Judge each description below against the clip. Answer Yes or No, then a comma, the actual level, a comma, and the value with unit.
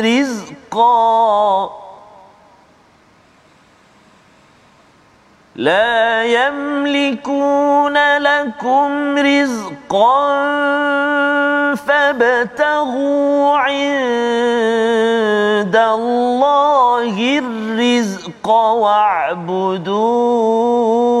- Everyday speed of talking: No, slow, 30 wpm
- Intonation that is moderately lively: Yes, average, 4.0 semitones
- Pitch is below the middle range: No, high, 245 Hz